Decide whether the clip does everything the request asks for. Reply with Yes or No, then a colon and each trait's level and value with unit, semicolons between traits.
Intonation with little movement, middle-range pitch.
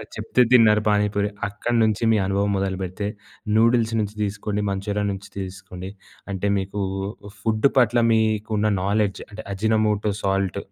No: narrow, 1.9 semitones; low, 105 Hz